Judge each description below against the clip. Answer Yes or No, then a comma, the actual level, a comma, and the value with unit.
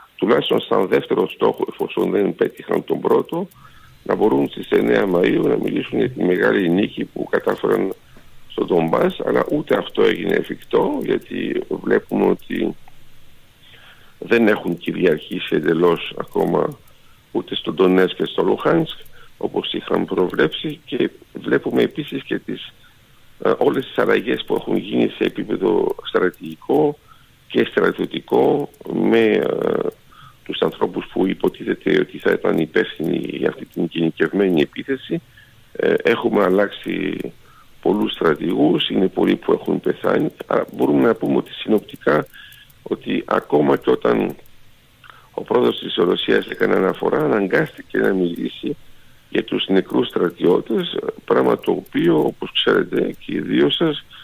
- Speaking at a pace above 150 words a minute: No, average, 130 wpm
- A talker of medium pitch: No, very high, 305 Hz